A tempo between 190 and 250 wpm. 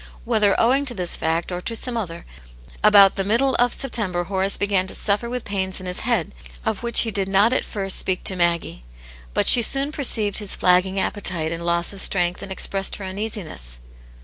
Yes: average, 200 wpm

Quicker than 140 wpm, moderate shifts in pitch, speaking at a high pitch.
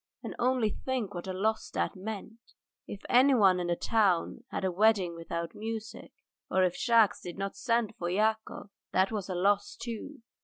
Yes: average, 180 wpm; average, 3.3 semitones; high, 205 Hz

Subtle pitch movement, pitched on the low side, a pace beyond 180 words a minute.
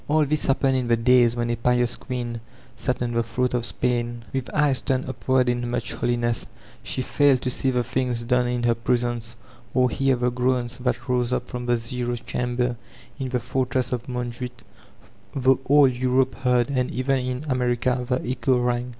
Yes: narrow, 1.1 semitones; low, 125 Hz; average, 190 wpm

